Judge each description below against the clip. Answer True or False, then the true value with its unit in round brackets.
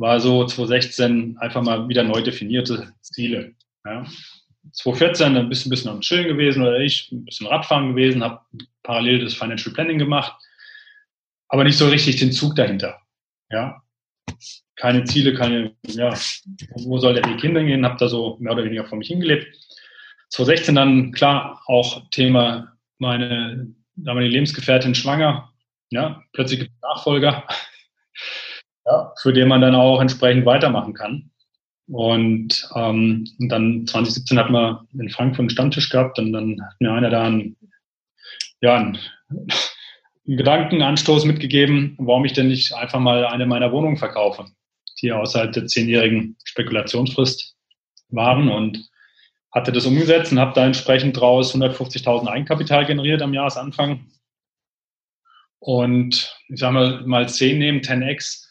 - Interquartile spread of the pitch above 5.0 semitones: False (2.8 semitones)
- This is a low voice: True (125 Hz)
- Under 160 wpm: True (145 wpm)